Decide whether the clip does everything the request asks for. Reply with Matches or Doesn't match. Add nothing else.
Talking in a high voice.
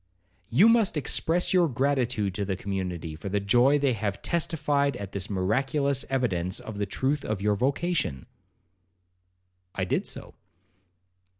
Doesn't match